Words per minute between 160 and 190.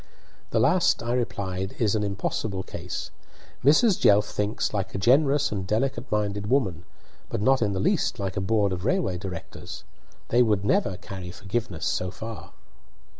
Yes: average, 165 wpm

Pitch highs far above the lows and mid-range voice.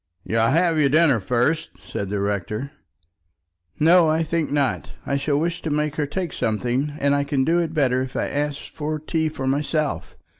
No: average, 3.2 semitones; medium, 145 Hz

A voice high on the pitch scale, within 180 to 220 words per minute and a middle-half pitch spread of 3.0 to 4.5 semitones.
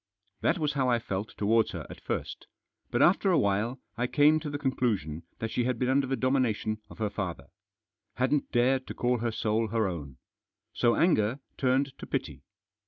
No: low, 120 Hz; average, 190 wpm; average, 3.7 semitones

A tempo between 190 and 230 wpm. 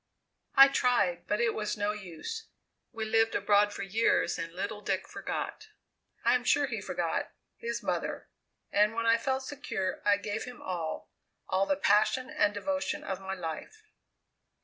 No: average, 165 wpm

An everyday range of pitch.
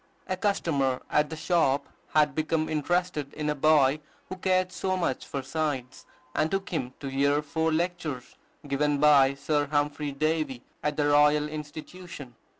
No: narrow, 2.3 semitones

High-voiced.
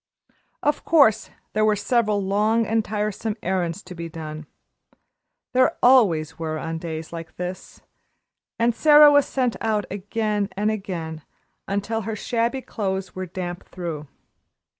Yes: high, 205 Hz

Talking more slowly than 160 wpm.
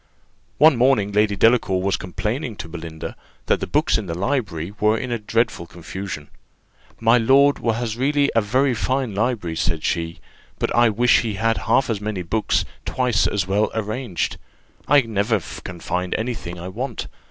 No: average, 170 wpm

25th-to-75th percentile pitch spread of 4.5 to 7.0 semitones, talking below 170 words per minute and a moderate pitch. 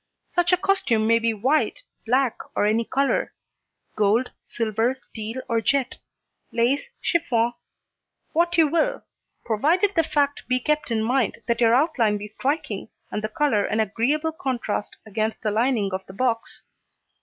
No: average, 5.0 semitones; average, 155 wpm; high, 240 Hz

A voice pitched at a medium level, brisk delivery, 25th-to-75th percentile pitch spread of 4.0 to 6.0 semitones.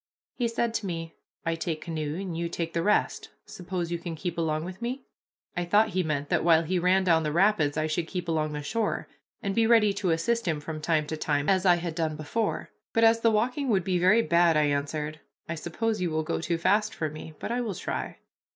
Yes: medium, 170 Hz; fast, 240 wpm; average, 4.5 semitones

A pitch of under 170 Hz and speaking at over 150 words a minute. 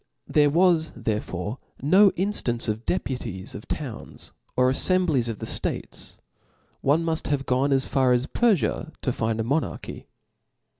Yes: low, 135 Hz; average, 160 wpm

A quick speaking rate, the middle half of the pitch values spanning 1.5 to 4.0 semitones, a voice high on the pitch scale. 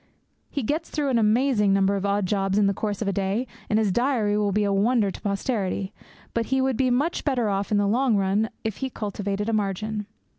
Yes: fast, 230 wpm; average, 3.5 semitones; high, 210 Hz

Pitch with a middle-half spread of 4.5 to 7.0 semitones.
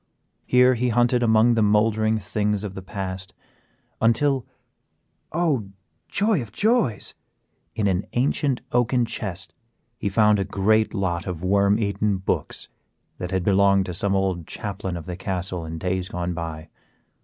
No: average, 3.6 semitones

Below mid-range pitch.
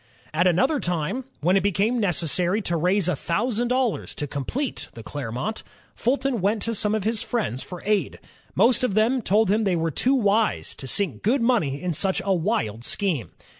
No: high, 200 Hz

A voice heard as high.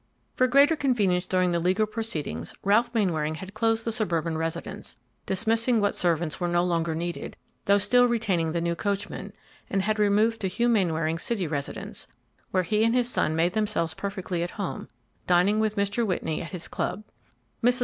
Yes: high, 195 Hz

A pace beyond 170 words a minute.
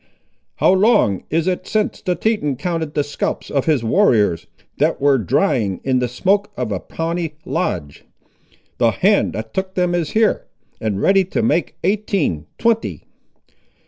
No: average, 155 wpm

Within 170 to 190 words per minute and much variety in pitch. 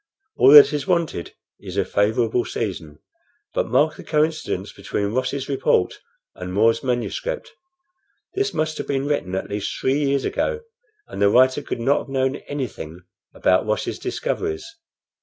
No: average, 155 wpm; wide, 5.9 semitones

